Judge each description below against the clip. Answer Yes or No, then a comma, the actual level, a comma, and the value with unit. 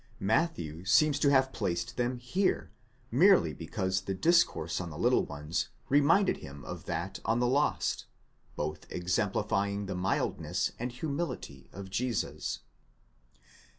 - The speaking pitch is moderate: No, low, 105 Hz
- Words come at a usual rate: No, slow, 125 wpm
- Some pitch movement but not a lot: No, wide, 7.4 semitones